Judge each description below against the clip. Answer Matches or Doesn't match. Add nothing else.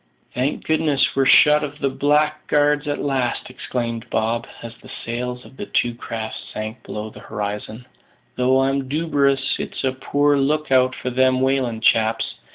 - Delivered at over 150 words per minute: Matches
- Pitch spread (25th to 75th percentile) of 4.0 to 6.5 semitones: Doesn't match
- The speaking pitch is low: Matches